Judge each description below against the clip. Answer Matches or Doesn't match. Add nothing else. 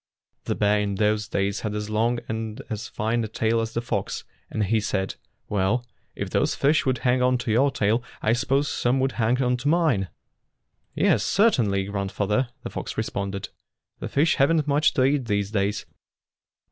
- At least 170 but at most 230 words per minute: Matches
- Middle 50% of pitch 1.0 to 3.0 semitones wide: Doesn't match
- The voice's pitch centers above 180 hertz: Doesn't match